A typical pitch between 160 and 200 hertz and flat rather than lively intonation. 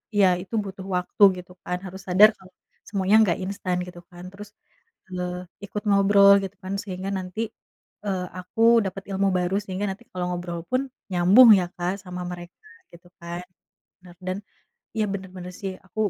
Yes: medium, 185 Hz; narrow, 1.8 semitones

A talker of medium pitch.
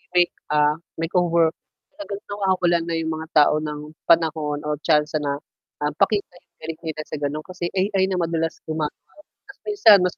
Yes: medium, 165 Hz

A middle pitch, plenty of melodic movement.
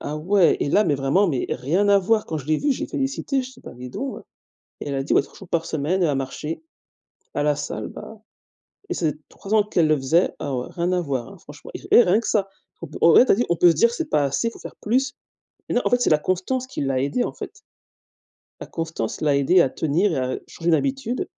Yes: medium, 170 Hz; wide, 6.9 semitones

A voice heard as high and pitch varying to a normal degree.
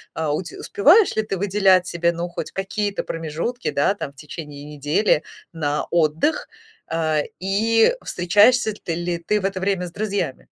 No: medium, 175 Hz; average, 4.3 semitones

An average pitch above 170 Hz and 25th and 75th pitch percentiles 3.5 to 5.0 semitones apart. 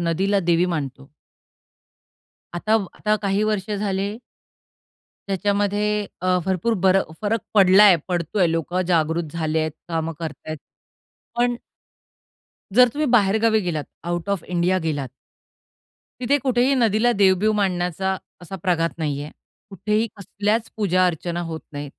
Yes: high, 190 Hz; average, 4.0 semitones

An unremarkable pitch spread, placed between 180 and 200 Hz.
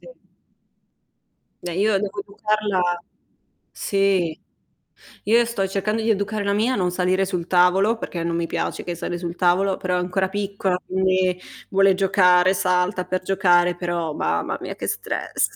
No: narrow, 2.0 semitones; medium, 185 Hz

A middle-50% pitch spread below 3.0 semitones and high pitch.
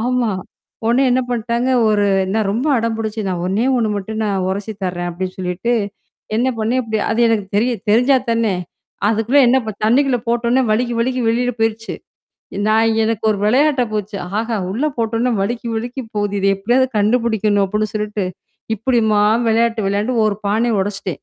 Yes: narrow, 2.6 semitones; high, 225 Hz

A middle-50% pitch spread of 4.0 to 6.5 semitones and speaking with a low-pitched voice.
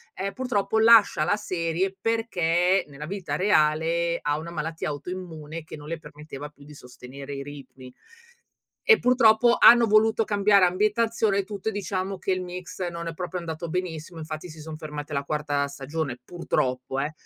No: average, 4.7 semitones; medium, 170 Hz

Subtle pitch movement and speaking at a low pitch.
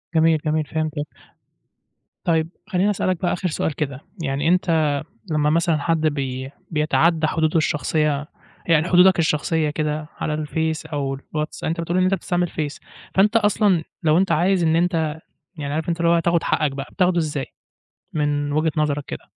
No: narrow, 2.2 semitones; medium, 160 Hz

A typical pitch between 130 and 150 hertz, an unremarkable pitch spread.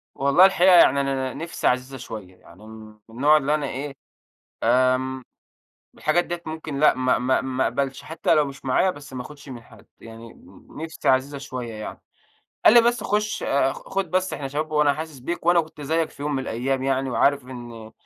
Yes: low, 135 Hz; average, 3.4 semitones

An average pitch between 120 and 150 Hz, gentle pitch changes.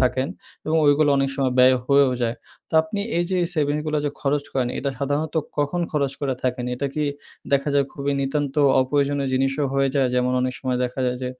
Yes: medium, 140 Hz; narrow, 2.0 semitones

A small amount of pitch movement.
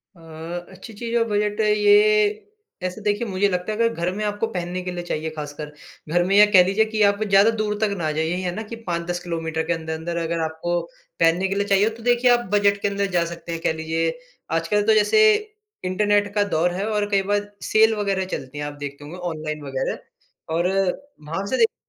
No: average, 3.9 semitones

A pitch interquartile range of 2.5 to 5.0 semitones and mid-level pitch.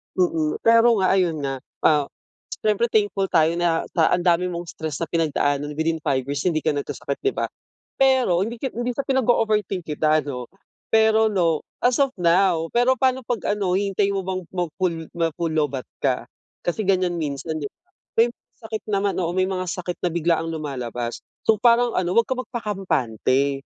No: wide, 5.4 semitones; medium, 180 Hz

